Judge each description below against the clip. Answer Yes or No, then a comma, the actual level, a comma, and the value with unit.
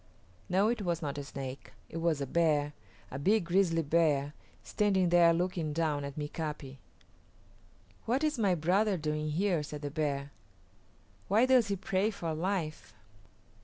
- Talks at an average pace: Yes, average, 155 wpm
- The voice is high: No, medium, 165 Hz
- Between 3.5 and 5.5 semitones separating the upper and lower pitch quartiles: Yes, average, 4.4 semitones